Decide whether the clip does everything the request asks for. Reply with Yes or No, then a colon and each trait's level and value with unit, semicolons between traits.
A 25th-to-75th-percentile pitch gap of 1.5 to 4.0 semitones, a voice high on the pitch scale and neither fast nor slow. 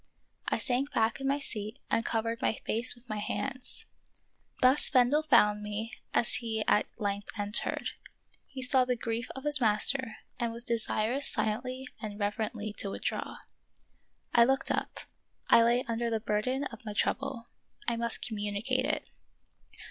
Yes: average, 3.1 semitones; high, 235 Hz; average, 155 wpm